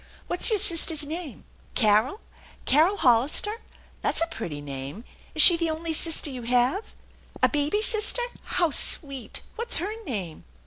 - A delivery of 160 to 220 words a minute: No, average, 150 wpm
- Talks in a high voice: Yes, very high, 305 Hz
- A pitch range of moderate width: No, wide, 6.7 semitones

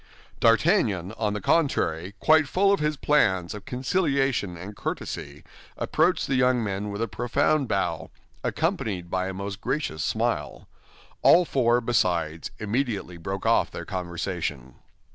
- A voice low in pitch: Yes, low, 105 Hz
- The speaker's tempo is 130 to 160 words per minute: Yes, average, 140 wpm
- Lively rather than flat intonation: Yes, wide, 6.8 semitones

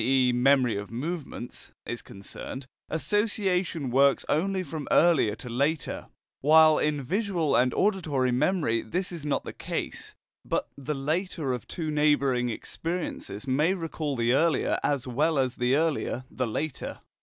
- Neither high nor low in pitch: Yes, medium, 145 Hz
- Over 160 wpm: No, average, 145 wpm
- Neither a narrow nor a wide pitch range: Yes, average, 4.5 semitones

